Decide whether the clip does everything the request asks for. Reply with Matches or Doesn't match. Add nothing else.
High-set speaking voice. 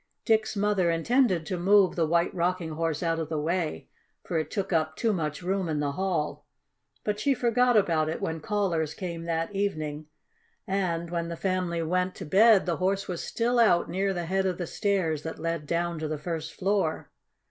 Doesn't match